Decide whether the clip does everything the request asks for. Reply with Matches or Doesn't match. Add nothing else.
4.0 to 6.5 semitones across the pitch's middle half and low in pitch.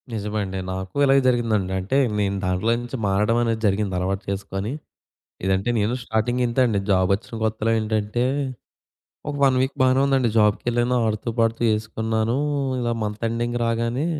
Doesn't match